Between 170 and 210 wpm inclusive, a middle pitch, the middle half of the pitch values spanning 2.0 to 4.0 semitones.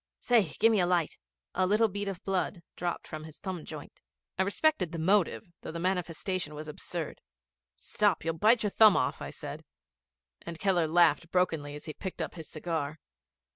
Yes: average, 180 wpm; medium, 175 Hz; average, 3.5 semitones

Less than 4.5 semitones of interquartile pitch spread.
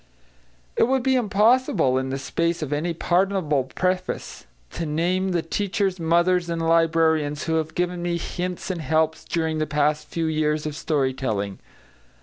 Yes: average, 3.1 semitones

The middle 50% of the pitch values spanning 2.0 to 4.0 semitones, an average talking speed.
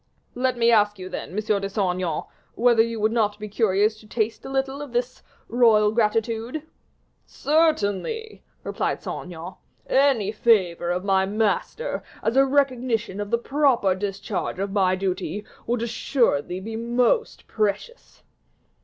Yes: average, 3.6 semitones; average, 150 wpm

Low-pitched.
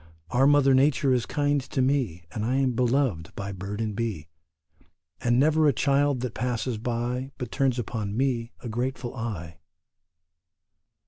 Yes: low, 125 Hz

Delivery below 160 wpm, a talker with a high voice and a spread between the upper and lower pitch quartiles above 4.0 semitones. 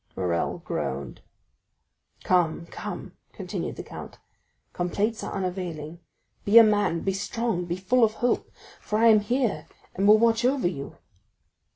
Yes: average, 145 wpm; high, 195 Hz; average, 4.7 semitones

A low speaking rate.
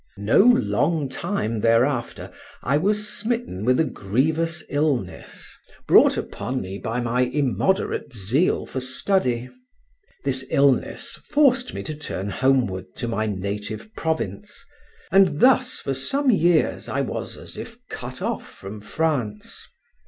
Yes: slow, 130 wpm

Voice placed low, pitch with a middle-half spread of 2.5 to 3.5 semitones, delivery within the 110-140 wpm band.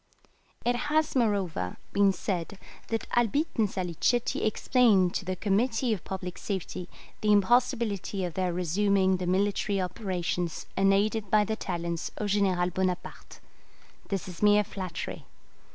No: high, 195 Hz; average, 2.9 semitones; slow, 135 wpm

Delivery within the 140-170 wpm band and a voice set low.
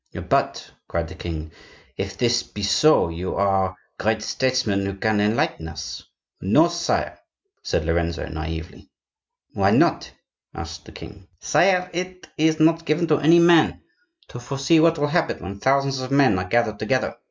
Yes: average, 160 wpm; low, 120 Hz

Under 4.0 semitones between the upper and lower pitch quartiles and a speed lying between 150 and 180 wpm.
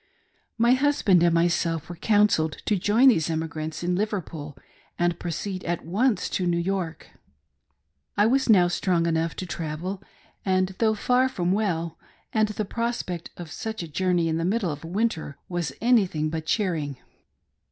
No: average, 4.3 semitones; average, 160 wpm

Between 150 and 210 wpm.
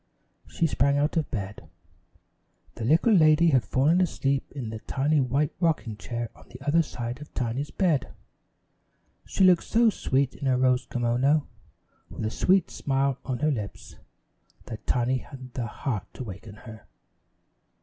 Yes: average, 160 wpm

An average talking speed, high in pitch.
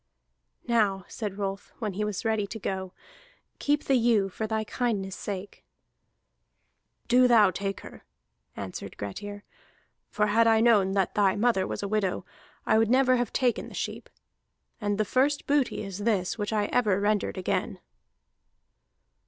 Yes: average, 155 wpm; high, 210 Hz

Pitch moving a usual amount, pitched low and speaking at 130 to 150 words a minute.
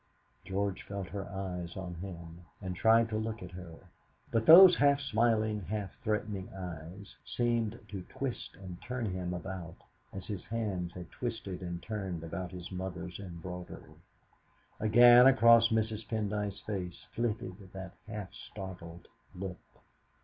Yes: average, 3.6 semitones; very low, 95 Hz; average, 140 wpm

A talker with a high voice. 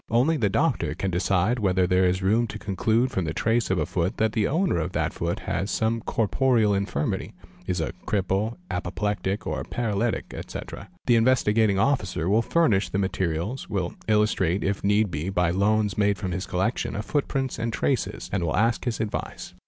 No: low, 105 Hz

